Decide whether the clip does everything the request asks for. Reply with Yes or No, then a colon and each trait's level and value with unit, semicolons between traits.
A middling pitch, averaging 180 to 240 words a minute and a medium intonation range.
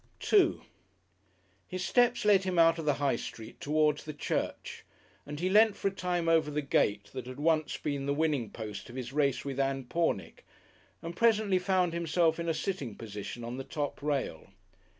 Yes: medium, 150 Hz; average, 190 wpm; average, 4.7 semitones